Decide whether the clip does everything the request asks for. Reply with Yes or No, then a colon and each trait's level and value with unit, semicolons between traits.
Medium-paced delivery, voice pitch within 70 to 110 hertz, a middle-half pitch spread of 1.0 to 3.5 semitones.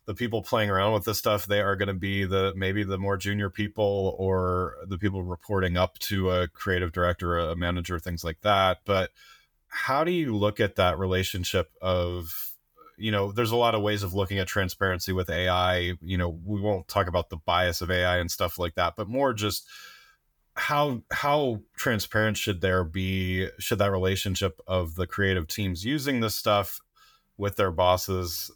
Yes: average, 190 wpm; very low, 95 Hz; narrow, 2.4 semitones